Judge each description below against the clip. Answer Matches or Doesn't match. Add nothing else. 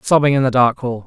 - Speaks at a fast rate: Matches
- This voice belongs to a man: Matches